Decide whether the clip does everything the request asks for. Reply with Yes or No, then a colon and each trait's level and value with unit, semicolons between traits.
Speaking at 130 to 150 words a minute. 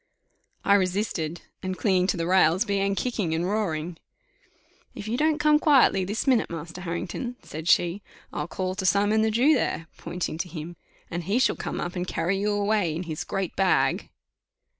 No: average, 185 wpm